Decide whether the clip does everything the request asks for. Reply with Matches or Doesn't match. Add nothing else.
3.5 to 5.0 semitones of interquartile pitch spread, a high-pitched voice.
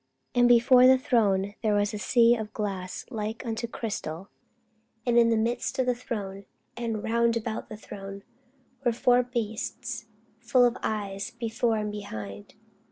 Doesn't match